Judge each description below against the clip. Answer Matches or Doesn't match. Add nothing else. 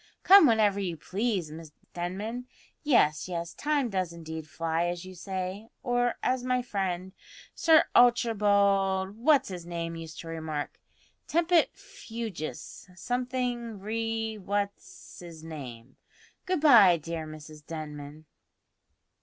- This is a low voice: Doesn't match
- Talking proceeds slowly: Matches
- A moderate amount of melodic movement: Doesn't match